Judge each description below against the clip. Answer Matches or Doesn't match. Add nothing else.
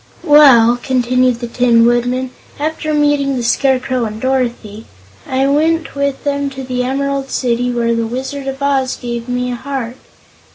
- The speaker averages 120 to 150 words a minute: Doesn't match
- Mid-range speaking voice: Doesn't match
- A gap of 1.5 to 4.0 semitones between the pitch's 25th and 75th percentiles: Matches